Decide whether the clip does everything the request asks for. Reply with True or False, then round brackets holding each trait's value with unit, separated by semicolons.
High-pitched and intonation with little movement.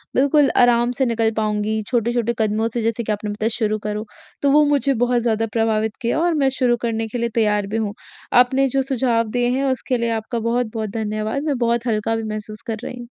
True (230 Hz; 2.3 semitones)